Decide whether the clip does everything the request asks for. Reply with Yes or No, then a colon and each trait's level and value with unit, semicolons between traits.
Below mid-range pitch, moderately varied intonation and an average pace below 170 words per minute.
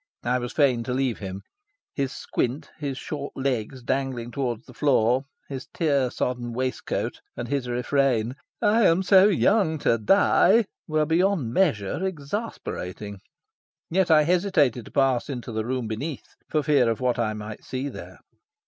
Yes: low, 130 Hz; average, 4.3 semitones; average, 155 wpm